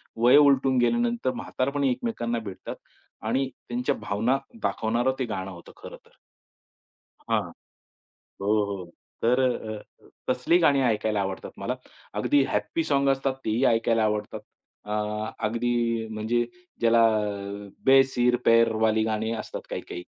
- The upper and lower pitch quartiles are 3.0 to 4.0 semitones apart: Yes, average, 3.4 semitones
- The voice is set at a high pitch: No, low, 115 Hz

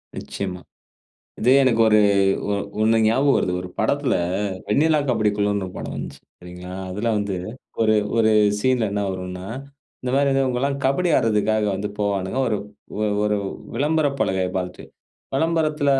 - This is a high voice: No, low, 110 Hz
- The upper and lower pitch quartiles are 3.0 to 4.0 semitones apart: No, average, 5.3 semitones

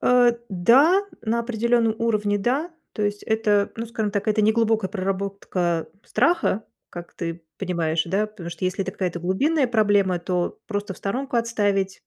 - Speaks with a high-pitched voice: Yes, high, 205 Hz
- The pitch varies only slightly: No, average, 3.6 semitones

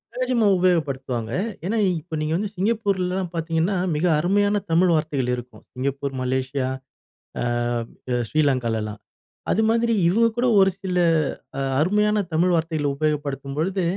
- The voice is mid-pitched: Yes, medium, 165 Hz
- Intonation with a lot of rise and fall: Yes, wide, 6.1 semitones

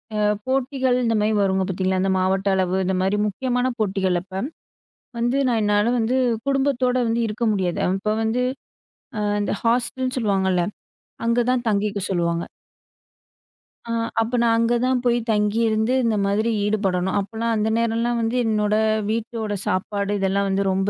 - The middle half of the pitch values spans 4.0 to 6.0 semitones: No, average, 3.5 semitones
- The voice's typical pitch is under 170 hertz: No, high, 215 Hz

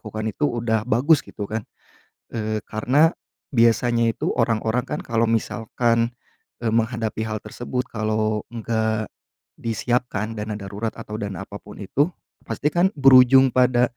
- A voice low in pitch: Yes, low, 115 Hz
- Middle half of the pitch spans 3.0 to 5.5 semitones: No, narrow, 2.4 semitones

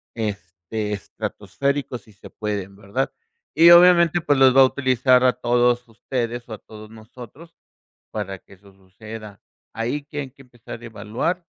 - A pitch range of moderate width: Yes, average, 4.1 semitones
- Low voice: Yes, low, 120 Hz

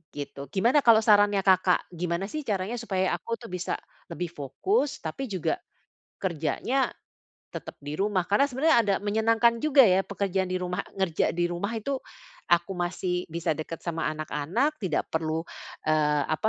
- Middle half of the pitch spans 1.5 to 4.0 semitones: No, average, 4.6 semitones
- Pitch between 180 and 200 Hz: Yes, high, 190 Hz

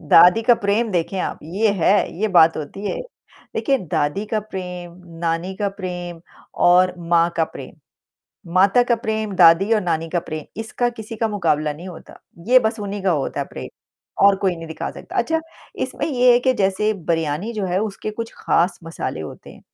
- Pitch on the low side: No, high, 190 Hz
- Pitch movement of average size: Yes, average, 4.5 semitones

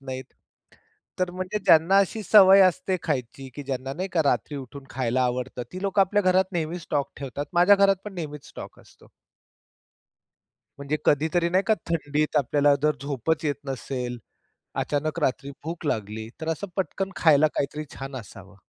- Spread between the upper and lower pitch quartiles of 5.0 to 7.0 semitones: Yes, average, 5.3 semitones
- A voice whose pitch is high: No, medium, 150 Hz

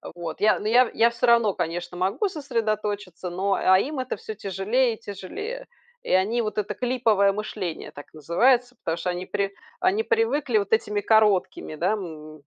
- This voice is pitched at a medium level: No, high, 210 Hz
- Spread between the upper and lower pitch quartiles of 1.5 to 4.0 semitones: No, average, 4.7 semitones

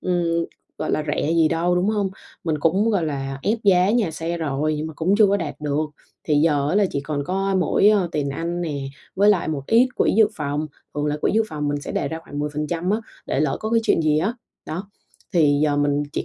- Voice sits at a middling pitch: Yes, medium, 160 Hz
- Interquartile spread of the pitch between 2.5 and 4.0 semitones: No, average, 4.4 semitones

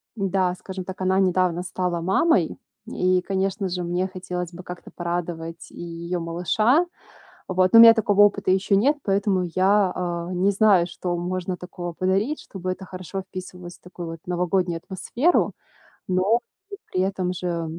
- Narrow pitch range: Yes, narrow, 1.6 semitones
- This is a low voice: No, medium, 185 Hz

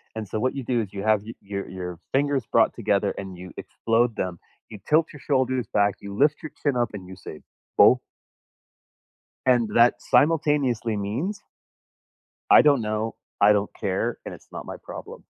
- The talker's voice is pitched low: Yes, low, 115 Hz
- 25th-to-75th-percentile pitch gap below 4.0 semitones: No, average, 5.0 semitones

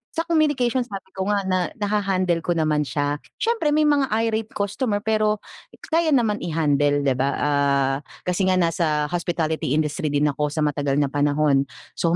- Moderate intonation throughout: No, wide, 6.3 semitones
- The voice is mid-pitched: Yes, medium, 170 Hz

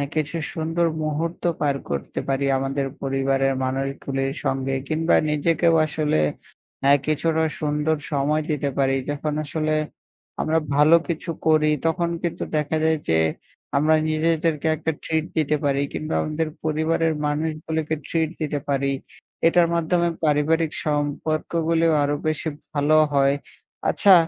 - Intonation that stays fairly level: Yes, narrow, 2.2 semitones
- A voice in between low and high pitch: Yes, medium, 155 Hz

